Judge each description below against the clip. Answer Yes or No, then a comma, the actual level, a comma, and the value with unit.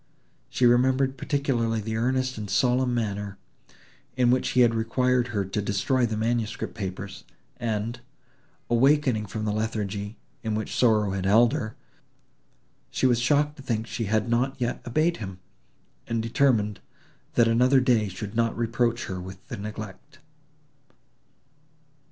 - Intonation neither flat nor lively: Yes, average, 3.0 semitones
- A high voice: No, low, 115 Hz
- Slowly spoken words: No, average, 145 wpm